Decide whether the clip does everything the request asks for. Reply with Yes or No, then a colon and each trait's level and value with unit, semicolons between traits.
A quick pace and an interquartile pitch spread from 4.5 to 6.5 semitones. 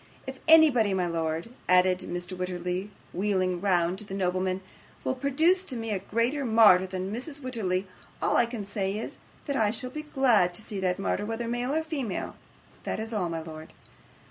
No: average, 185 wpm; average, 5.3 semitones